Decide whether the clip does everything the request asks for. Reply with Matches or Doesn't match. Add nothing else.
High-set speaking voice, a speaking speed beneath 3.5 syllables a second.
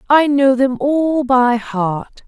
Matches